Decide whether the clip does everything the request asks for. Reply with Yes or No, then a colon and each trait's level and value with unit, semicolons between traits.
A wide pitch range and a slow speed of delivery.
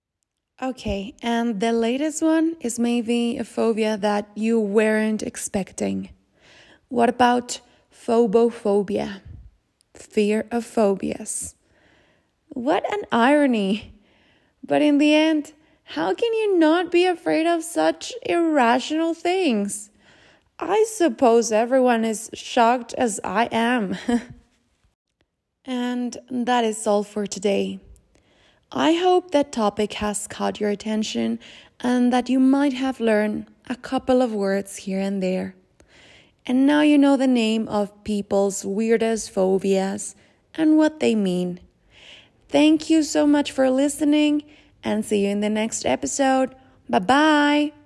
Yes: wide, 5.7 semitones; slow, 125 wpm